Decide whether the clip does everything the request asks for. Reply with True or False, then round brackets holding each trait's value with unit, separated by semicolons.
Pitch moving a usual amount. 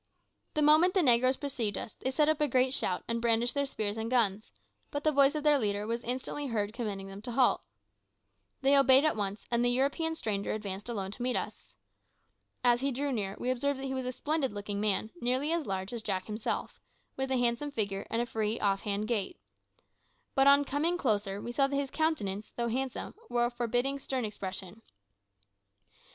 True (4.6 semitones)